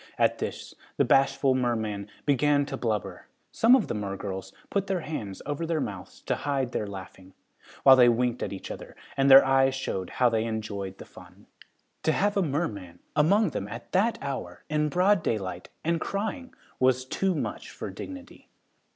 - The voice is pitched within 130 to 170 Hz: Yes, low, 135 Hz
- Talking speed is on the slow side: No, average, 175 wpm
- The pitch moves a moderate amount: No, wide, 7.2 semitones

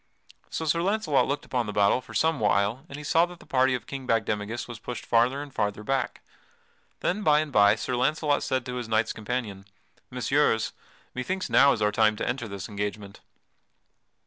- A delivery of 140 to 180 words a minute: No, average, 195 wpm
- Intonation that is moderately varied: Yes, average, 5.0 semitones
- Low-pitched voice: Yes, low, 125 Hz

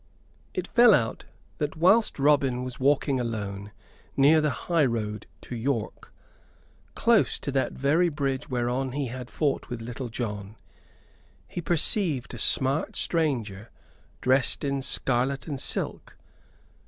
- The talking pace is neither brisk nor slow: No, slow, 130 wpm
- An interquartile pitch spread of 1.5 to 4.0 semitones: Yes, average, 3.6 semitones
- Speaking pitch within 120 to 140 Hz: Yes, low, 135 Hz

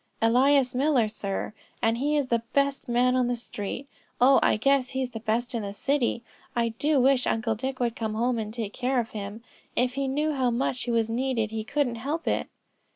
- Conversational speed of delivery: No, fast, 215 wpm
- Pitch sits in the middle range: No, high, 245 Hz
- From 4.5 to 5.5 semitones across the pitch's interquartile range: No, average, 2.9 semitones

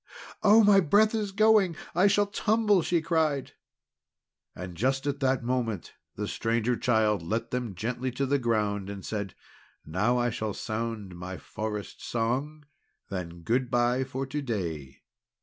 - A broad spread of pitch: Yes, wide, 6.1 semitones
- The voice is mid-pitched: No, low, 120 Hz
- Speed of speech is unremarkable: Yes, average, 155 wpm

